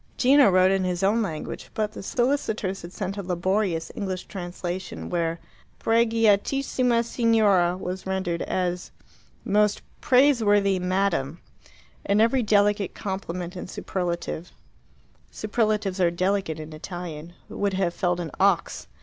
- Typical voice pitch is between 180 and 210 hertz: Yes, high, 190 Hz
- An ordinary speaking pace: No, slow, 125 wpm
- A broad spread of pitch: No, average, 3.2 semitones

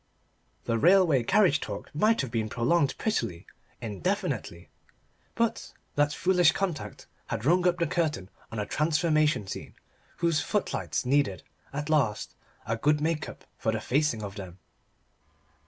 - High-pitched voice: No, medium, 145 Hz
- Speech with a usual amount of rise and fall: No, wide, 7.0 semitones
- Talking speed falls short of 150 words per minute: Yes, average, 140 wpm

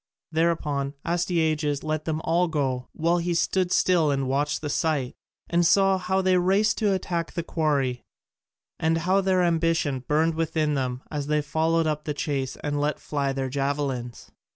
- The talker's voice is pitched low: No, medium, 155 Hz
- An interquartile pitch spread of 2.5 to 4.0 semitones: Yes, average, 3.1 semitones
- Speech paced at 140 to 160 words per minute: No, average, 170 wpm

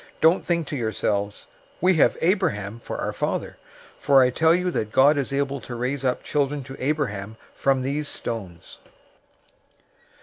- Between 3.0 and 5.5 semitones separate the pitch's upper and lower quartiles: Yes, average, 4.5 semitones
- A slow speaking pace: No, average, 165 wpm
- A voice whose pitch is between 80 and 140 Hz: Yes, low, 135 Hz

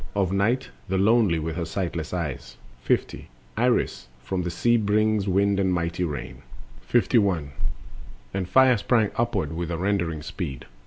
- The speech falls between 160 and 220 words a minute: Yes, average, 165 wpm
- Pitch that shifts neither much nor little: Yes, average, 3.7 semitones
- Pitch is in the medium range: No, very low, 95 Hz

